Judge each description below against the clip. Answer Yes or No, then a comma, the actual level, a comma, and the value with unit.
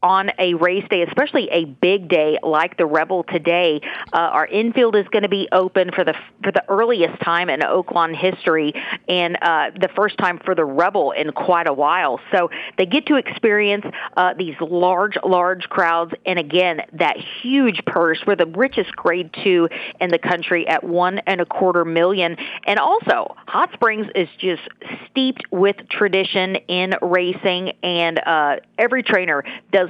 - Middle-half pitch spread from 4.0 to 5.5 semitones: No, average, 2.9 semitones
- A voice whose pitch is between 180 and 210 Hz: Yes, medium, 185 Hz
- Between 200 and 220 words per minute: No, average, 175 wpm